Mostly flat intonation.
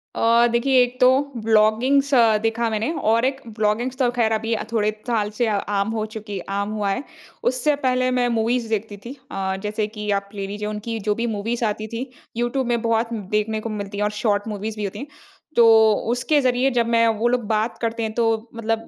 Yes: narrow, 2.3 semitones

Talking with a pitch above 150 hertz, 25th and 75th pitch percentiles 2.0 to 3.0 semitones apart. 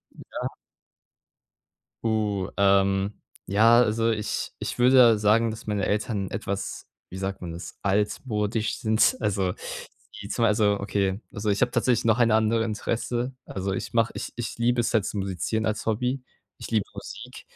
No: low, 110 Hz; narrow, 2.5 semitones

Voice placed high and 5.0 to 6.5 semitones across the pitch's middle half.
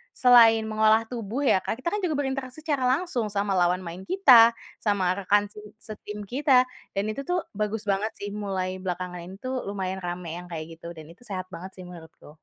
Yes: high, 210 Hz; average, 5.3 semitones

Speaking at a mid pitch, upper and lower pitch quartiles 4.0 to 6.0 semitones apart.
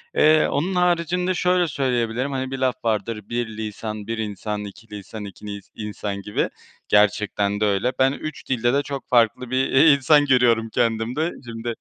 No: low, 120 Hz; average, 4.6 semitones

